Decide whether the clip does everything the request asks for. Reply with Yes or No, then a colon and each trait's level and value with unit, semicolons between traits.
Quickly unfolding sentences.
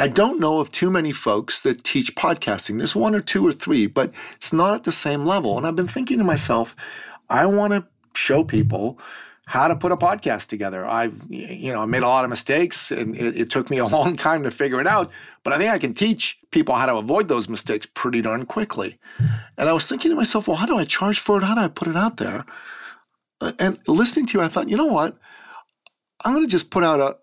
Yes: fast, 245 wpm